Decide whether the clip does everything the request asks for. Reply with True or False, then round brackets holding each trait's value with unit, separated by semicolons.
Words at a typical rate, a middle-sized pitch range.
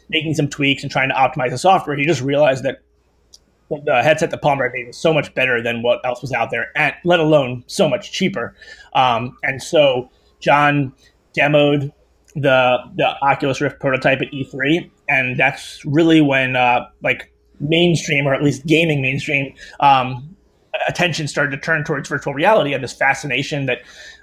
True (175 wpm; 3.0 semitones)